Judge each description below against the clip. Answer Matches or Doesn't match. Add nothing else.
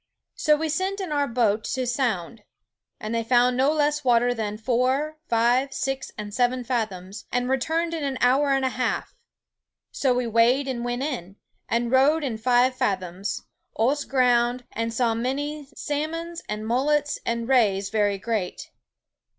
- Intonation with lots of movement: Doesn't match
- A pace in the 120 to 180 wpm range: Matches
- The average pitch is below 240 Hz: Doesn't match